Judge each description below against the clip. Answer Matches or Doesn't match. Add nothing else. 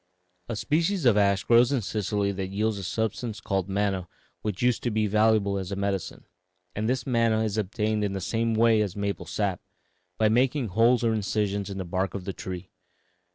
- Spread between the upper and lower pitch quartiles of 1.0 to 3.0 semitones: Matches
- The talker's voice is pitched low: Matches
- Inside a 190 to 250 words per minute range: Matches